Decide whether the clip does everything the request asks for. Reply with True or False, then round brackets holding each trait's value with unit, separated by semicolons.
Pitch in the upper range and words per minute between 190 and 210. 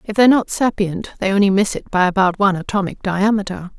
True (200 Hz; 205 wpm)